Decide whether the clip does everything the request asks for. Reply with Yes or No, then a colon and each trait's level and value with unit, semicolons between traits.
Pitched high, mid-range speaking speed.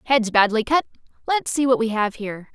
Yes: high, 240 Hz; average, 190 wpm